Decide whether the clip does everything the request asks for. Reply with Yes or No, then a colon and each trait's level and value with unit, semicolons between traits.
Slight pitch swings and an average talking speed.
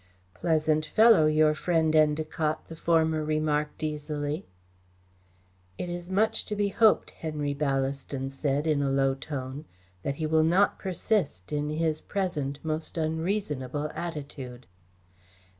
No: narrow, 2.2 semitones; slow, 125 wpm